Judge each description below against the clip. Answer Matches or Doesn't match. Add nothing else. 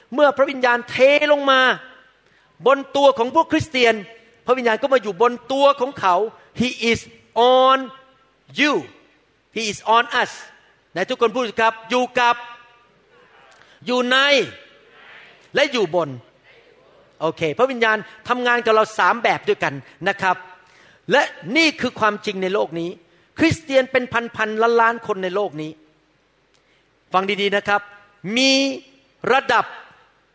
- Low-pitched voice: Doesn't match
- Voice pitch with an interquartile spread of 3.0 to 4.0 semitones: Doesn't match